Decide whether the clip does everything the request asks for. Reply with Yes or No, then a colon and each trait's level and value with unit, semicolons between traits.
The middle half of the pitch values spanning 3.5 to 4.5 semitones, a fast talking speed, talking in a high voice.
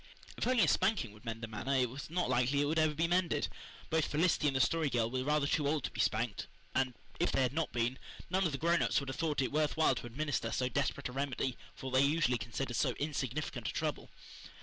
No: average, 3.9 semitones; fast, 250 wpm; medium, 140 Hz